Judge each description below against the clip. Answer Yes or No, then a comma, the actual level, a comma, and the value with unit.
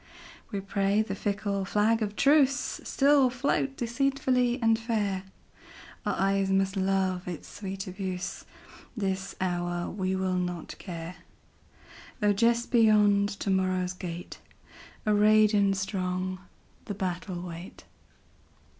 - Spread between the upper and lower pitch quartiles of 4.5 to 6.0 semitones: No, narrow, 2.6 semitones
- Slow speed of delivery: Yes, slow, 100 wpm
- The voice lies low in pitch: No, high, 195 Hz